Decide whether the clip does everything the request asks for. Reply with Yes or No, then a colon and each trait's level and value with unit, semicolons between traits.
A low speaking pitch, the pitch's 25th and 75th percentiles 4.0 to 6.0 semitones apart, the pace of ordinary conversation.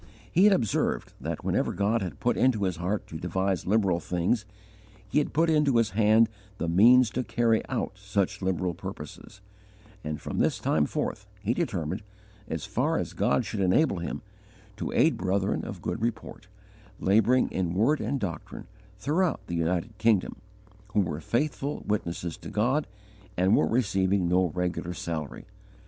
Yes: low, 100 Hz; average, 4.5 semitones; average, 160 wpm